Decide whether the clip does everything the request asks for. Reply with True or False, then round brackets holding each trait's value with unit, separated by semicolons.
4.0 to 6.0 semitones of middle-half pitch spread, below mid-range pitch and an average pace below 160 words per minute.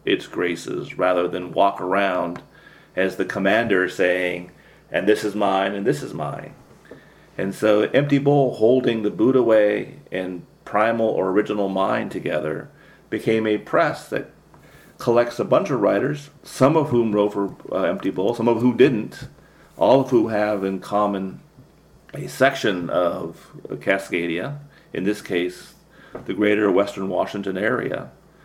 False (3.5 semitones; 105 Hz; 150 wpm)